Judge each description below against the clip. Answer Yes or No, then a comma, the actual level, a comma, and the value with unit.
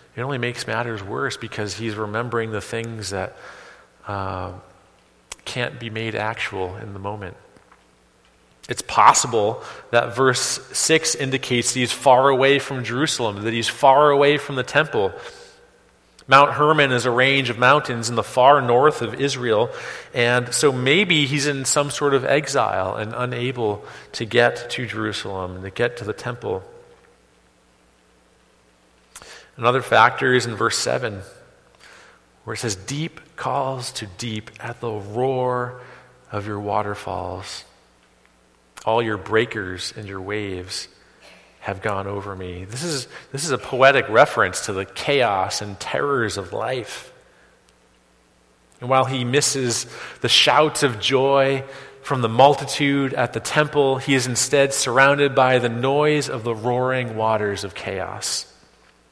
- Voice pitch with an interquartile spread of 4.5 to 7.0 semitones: Yes, average, 4.9 semitones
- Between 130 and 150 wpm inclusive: Yes, average, 145 wpm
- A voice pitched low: Yes, low, 120 Hz